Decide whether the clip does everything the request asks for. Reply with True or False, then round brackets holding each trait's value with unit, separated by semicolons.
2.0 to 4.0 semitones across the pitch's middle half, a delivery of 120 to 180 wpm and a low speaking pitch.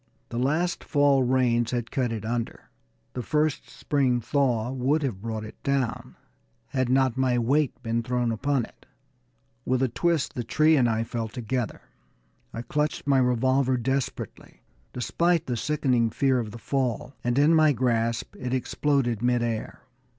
True (2.8 semitones; 165 wpm; 125 Hz)